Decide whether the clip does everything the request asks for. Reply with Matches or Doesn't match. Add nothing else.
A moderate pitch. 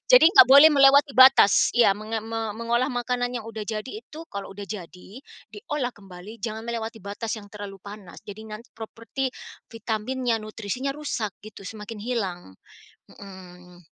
Doesn't match